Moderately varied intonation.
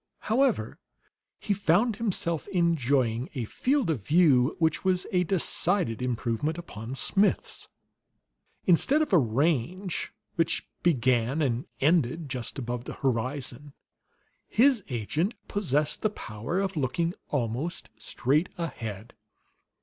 No: wide, 6.5 semitones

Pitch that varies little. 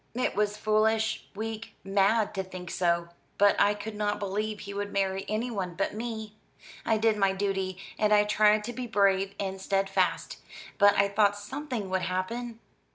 Yes: narrow, 2.0 semitones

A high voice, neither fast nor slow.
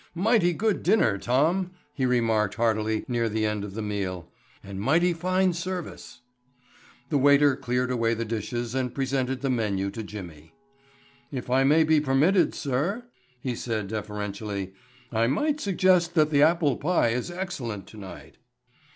No: low, 125 Hz; average, 150 wpm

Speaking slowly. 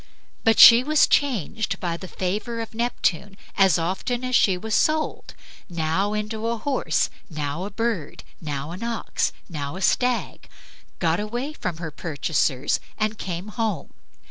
No: average, 155 wpm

